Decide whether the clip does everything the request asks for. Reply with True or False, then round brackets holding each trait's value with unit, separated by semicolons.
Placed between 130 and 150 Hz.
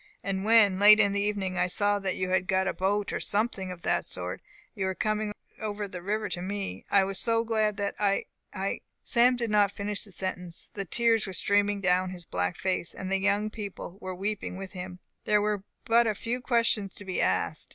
False (200 Hz)